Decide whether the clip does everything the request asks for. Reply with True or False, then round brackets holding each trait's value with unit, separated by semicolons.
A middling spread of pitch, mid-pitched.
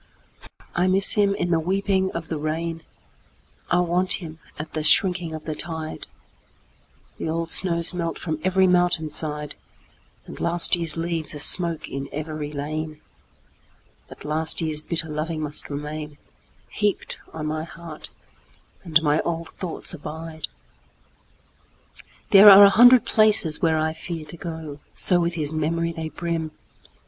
False (2.1 semitones; 165 Hz)